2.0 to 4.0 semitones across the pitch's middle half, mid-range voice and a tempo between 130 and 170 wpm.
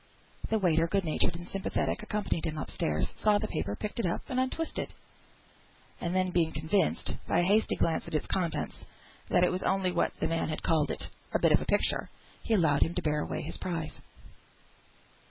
No: average, 3.7 semitones; medium, 175 Hz; average, 200 wpm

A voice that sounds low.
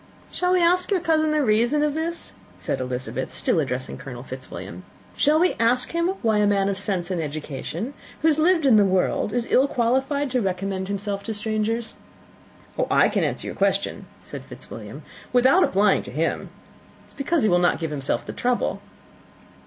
No: high, 220 Hz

